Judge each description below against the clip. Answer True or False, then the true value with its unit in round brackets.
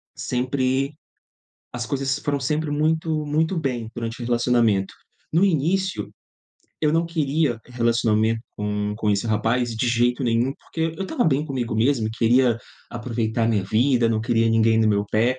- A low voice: True (120 Hz)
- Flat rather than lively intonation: False (4.3 semitones)